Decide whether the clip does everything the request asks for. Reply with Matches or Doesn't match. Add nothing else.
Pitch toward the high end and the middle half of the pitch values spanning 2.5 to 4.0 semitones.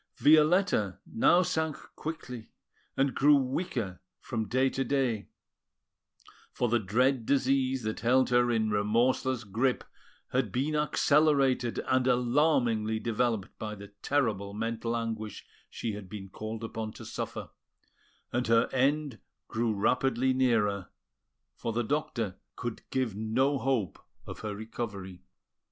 Doesn't match